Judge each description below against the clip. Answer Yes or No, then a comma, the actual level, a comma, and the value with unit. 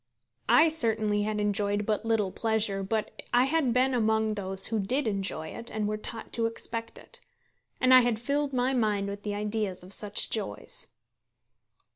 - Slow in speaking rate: No, average, 175 wpm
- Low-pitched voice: No, high, 220 Hz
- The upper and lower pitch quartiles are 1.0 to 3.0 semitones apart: Yes, average, 2.7 semitones